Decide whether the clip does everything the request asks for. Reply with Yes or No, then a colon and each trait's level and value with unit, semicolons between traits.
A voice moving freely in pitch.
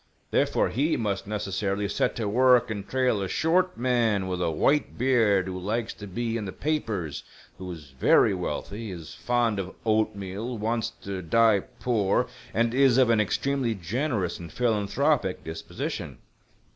No: average, 3.9 semitones